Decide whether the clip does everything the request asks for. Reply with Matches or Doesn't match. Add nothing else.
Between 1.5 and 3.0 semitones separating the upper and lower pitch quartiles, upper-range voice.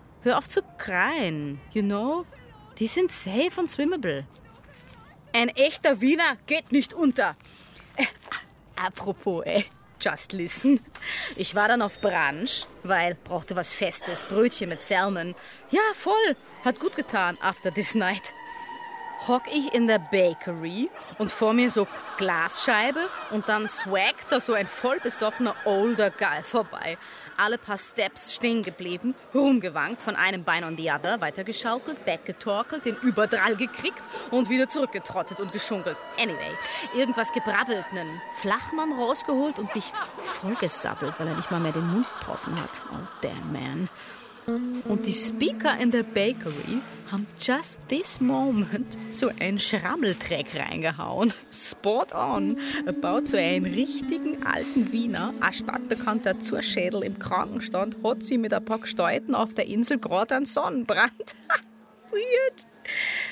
Doesn't match